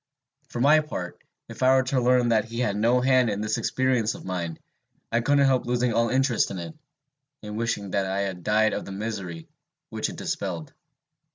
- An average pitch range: Yes, average, 4.1 semitones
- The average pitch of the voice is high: No, low, 115 Hz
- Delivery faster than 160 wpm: Yes, average, 200 wpm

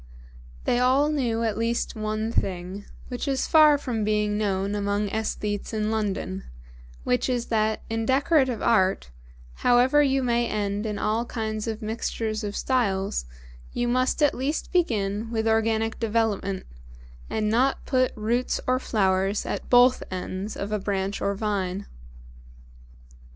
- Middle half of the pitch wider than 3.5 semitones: No, average, 3.2 semitones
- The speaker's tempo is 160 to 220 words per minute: No, average, 145 wpm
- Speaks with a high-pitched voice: Yes, high, 220 Hz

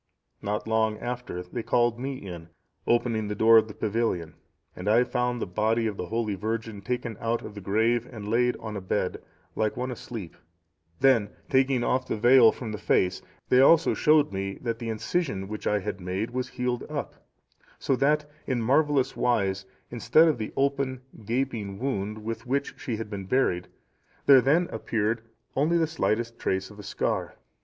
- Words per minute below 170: No, average, 180 wpm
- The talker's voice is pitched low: Yes, low, 115 Hz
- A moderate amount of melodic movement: Yes, average, 3.4 semitones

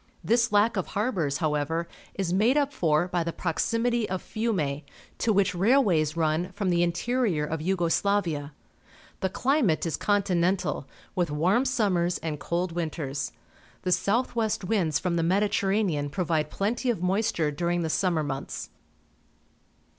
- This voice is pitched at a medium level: Yes, medium, 180 Hz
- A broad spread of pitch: No, average, 4.3 semitones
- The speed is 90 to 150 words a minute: Yes, average, 145 wpm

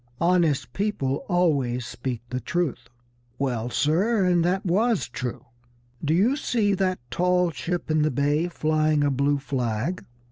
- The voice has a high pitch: No, medium, 155 Hz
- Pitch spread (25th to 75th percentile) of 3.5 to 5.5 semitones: Yes, average, 5.1 semitones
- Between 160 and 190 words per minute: No, average, 145 wpm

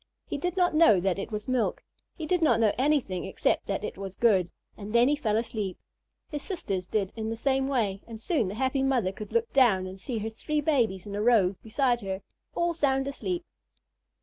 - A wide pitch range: Yes, wide, 5.9 semitones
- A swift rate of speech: Yes, fast, 215 wpm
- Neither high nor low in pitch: No, high, 230 Hz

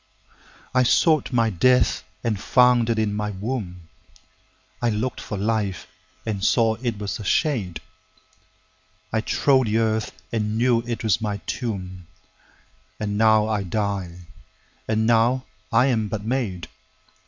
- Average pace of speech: No, slow, 130 wpm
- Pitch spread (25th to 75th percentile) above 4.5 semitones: No, average, 3.8 semitones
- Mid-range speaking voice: No, low, 105 Hz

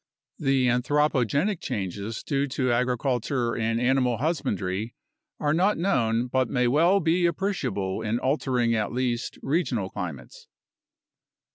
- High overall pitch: No, low, 125 Hz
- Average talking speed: No, slow, 120 wpm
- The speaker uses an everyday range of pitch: Yes, average, 4.3 semitones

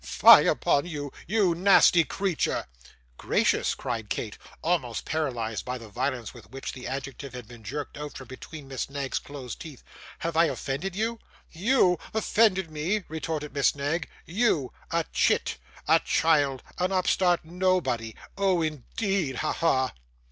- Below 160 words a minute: Yes, average, 150 wpm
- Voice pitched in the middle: Yes, medium, 155 Hz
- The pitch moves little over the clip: No, average, 5.1 semitones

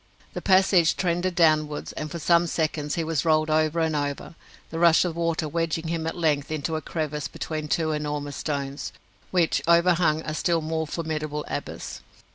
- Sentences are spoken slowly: No, average, 175 wpm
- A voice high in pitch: No, medium, 160 Hz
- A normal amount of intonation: No, narrow, 1.8 semitones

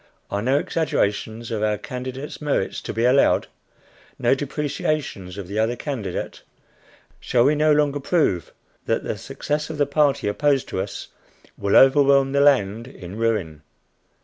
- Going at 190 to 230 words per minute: No, average, 150 wpm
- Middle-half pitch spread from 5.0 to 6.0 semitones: Yes, average, 5.3 semitones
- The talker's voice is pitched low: Yes, low, 130 Hz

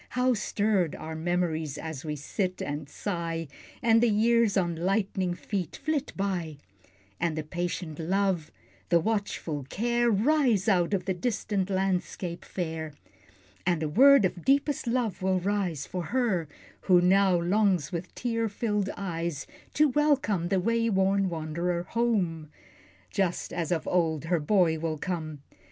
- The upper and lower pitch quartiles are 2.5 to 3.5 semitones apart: No, average, 4.2 semitones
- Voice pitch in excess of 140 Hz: Yes, medium, 185 Hz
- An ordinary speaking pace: Yes, average, 145 wpm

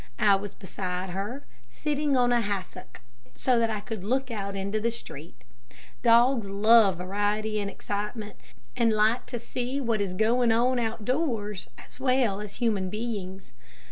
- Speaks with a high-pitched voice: Yes, high, 215 Hz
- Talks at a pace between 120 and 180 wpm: Yes, average, 160 wpm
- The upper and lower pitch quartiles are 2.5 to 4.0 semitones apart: Yes, average, 3.3 semitones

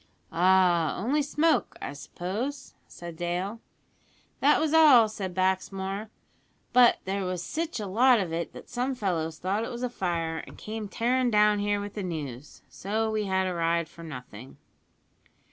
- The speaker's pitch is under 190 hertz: No, high, 195 Hz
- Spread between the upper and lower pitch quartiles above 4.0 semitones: Yes, average, 5.2 semitones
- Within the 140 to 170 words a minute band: Yes, average, 165 wpm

